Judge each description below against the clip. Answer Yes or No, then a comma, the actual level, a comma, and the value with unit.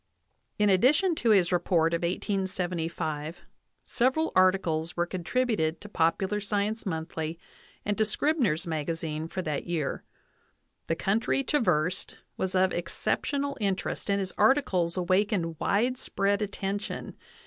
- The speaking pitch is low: No, medium, 185 Hz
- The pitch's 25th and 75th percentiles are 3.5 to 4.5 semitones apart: Yes, average, 4.0 semitones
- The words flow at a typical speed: No, slow, 125 wpm